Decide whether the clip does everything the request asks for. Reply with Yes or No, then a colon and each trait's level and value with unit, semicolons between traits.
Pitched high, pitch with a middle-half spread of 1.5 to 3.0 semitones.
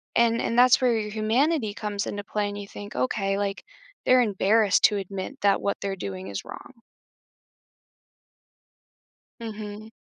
Yes: high, 210 Hz; narrow, 2.4 semitones